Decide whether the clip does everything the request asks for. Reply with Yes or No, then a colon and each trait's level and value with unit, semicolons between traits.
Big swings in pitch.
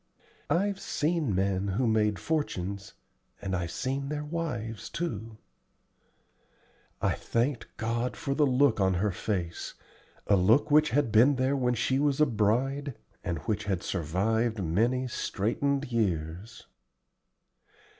Yes: wide, 5.9 semitones